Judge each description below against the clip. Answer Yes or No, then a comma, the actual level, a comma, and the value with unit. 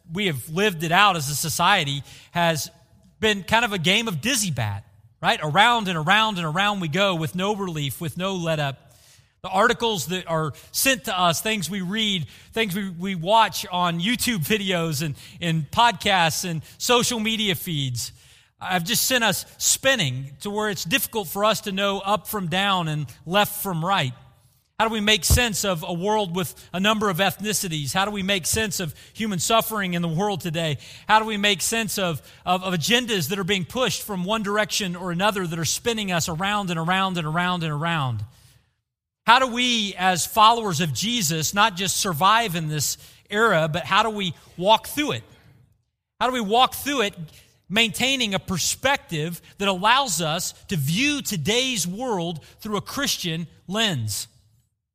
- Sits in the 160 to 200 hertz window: Yes, medium, 185 Hz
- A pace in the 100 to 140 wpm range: No, average, 185 wpm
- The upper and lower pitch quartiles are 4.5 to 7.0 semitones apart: Yes, average, 5.3 semitones